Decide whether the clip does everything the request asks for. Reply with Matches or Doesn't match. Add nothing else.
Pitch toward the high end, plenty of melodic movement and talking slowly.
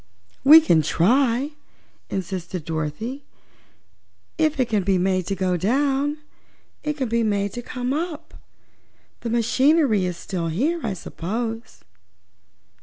Matches